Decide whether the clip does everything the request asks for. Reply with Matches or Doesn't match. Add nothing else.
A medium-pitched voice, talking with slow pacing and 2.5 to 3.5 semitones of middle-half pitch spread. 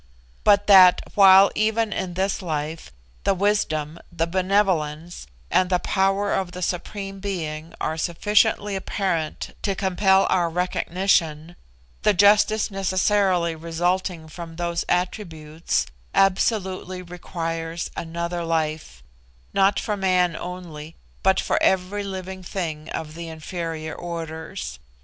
Matches